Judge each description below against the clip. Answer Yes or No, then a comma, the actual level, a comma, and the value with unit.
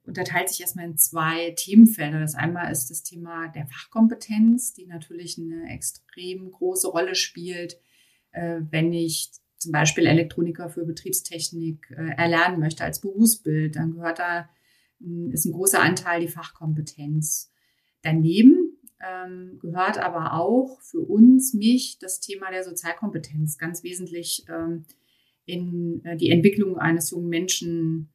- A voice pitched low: No, medium, 170 Hz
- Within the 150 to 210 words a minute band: No, slow, 125 wpm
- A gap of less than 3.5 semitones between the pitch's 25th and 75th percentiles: Yes, narrow, 2.4 semitones